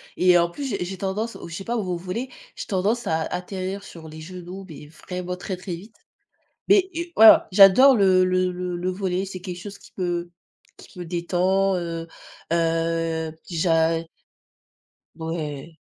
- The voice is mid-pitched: Yes, medium, 180 Hz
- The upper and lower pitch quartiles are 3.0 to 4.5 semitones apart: No, narrow, 2.5 semitones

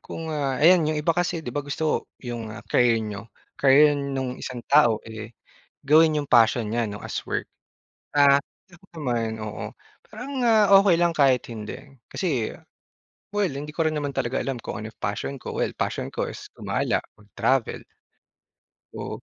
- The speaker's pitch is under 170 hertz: Yes, medium, 140 Hz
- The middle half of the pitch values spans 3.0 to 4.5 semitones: No, average, 5.3 semitones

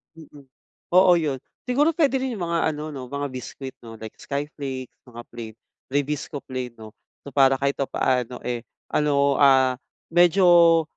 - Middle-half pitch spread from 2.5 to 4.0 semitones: No, average, 4.4 semitones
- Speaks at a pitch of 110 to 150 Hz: Yes, medium, 140 Hz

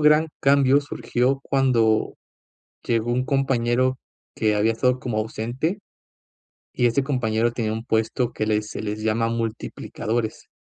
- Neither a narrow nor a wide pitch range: Yes, average, 3.0 semitones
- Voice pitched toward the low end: Yes, low, 120 Hz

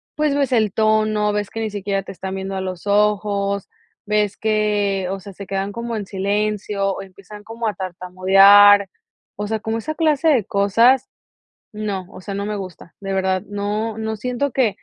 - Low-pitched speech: No, high, 205 Hz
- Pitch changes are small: Yes, narrow, 2.0 semitones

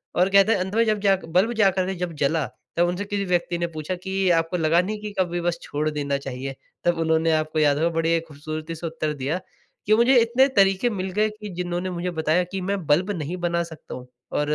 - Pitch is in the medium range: Yes, medium, 175 Hz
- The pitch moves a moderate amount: Yes, average, 3.6 semitones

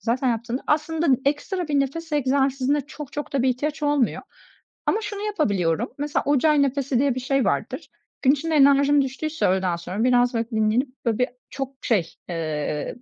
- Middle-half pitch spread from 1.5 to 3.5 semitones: No, average, 3.9 semitones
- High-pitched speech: Yes, very high, 270 Hz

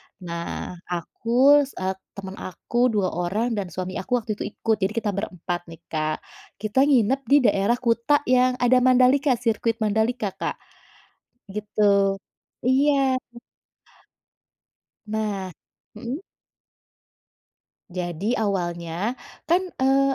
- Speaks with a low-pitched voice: No, high, 220 Hz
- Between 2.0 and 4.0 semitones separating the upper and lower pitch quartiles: No, average, 4.9 semitones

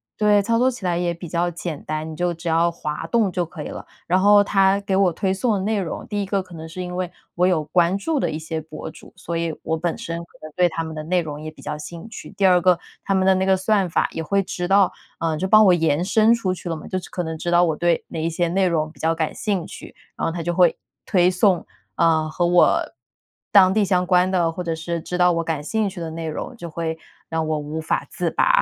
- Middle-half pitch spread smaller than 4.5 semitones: Yes, average, 2.8 semitones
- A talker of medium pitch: Yes, medium, 175 Hz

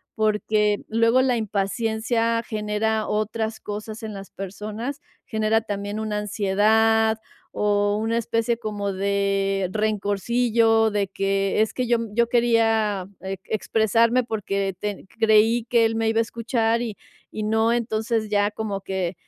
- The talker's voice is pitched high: Yes, high, 220 Hz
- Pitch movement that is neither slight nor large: No, narrow, 1.8 semitones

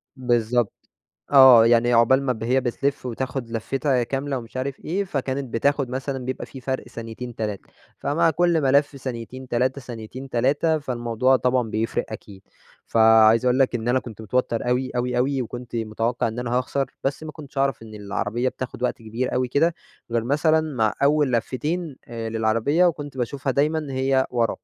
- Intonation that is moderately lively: Yes, average, 3.0 semitones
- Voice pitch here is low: Yes, low, 125 Hz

